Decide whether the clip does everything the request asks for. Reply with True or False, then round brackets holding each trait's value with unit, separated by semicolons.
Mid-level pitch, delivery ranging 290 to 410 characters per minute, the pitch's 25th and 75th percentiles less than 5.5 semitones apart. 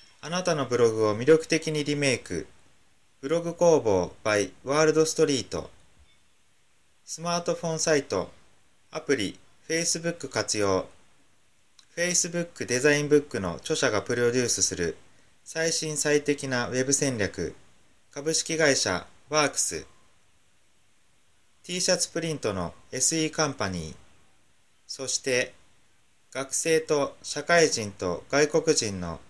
False (145 Hz; 265 characters per minute; 5.1 semitones)